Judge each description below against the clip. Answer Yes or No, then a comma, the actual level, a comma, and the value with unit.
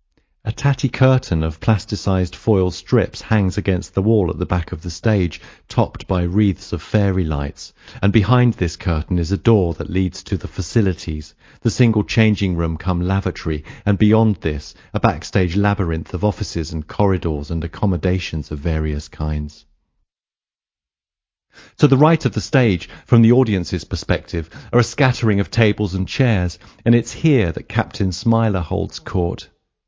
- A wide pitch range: No, average, 4.7 semitones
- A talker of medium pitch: No, very low, 95 Hz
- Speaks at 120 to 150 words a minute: No, average, 165 wpm